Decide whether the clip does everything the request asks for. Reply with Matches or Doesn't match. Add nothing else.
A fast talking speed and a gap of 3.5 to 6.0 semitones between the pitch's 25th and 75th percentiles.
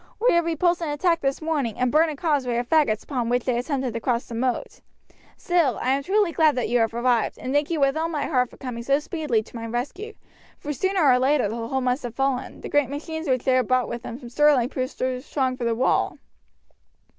Matches